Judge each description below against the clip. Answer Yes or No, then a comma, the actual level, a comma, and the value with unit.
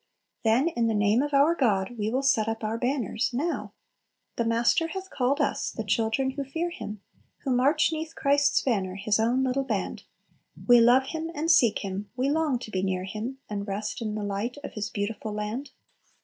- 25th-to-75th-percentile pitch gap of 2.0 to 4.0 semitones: No, average, 4.6 semitones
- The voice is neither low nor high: No, high, 235 Hz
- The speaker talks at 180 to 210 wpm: Yes, average, 200 wpm